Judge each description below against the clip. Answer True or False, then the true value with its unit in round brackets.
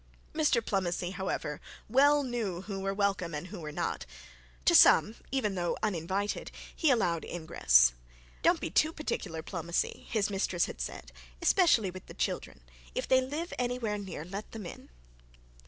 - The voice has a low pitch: False (195 Hz)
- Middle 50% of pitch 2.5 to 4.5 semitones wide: False (5.6 semitones)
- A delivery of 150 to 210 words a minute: True (155 wpm)